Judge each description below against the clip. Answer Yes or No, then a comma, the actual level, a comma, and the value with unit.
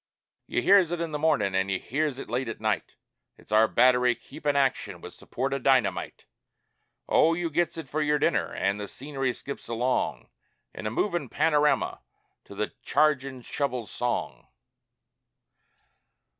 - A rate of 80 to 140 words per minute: No, average, 155 wpm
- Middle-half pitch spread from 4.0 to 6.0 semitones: Yes, average, 4.4 semitones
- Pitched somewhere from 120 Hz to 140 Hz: Yes, low, 135 Hz